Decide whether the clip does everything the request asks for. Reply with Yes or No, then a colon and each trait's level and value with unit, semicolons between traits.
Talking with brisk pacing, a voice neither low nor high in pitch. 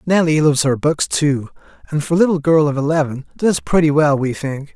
Yes: fast, 215 wpm; medium, 150 Hz